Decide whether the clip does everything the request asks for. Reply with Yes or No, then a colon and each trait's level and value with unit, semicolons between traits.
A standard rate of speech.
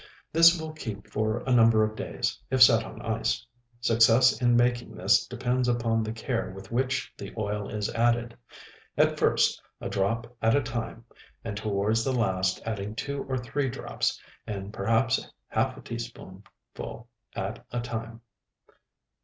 Yes: average, 155 wpm